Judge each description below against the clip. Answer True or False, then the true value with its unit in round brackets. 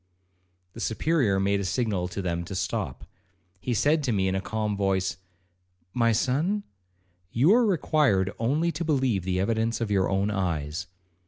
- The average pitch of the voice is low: True (105 Hz)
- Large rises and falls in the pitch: True (5.8 semitones)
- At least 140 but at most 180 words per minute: True (165 wpm)